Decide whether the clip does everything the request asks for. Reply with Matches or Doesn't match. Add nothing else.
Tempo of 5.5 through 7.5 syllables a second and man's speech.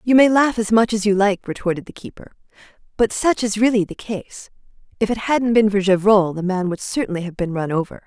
Doesn't match